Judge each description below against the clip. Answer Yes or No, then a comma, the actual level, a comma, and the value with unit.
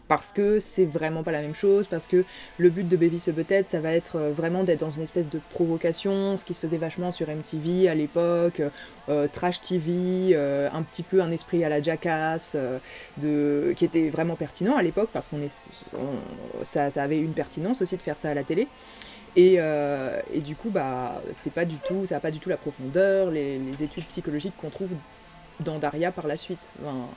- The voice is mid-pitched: Yes, medium, 165 Hz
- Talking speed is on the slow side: No, average, 215 wpm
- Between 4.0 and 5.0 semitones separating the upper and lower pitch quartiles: No, average, 3.0 semitones